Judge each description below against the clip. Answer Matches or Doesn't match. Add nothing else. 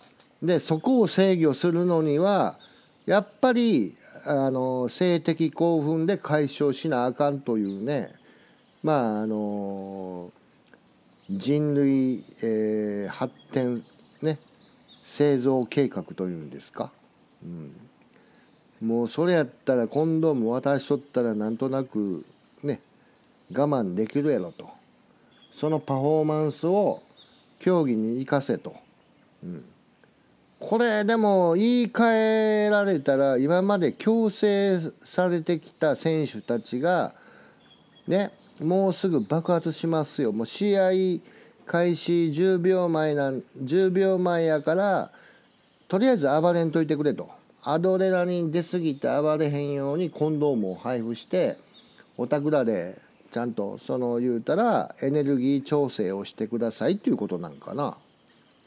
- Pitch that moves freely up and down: Matches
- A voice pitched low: Doesn't match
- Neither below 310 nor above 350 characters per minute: Doesn't match